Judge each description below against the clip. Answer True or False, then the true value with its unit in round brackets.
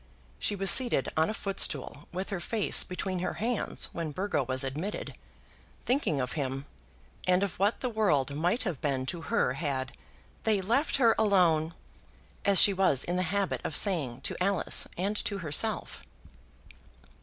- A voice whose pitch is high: False (180 Hz)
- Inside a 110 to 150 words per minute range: False (165 wpm)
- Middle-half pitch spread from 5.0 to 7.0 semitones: True (5.6 semitones)